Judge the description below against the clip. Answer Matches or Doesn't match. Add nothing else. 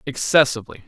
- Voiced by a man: Matches